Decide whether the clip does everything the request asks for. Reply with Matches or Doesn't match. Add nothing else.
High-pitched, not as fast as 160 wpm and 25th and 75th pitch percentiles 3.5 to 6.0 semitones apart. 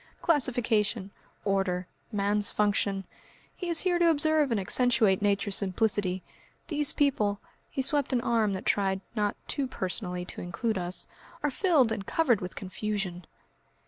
Matches